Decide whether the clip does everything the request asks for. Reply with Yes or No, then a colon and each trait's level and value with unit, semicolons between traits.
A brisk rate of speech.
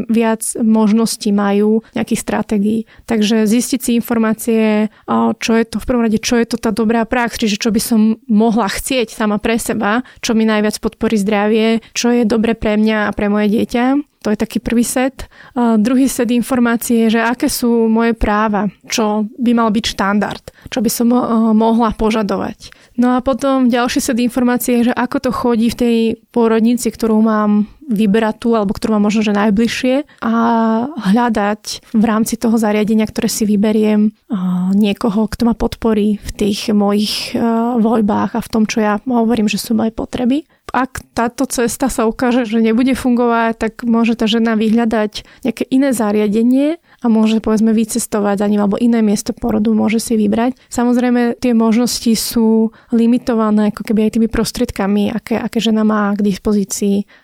Yes: fast, 175 wpm